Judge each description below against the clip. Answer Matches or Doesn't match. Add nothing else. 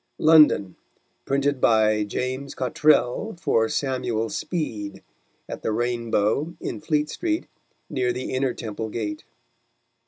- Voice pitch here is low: Matches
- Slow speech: Matches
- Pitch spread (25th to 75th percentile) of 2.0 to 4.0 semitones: Doesn't match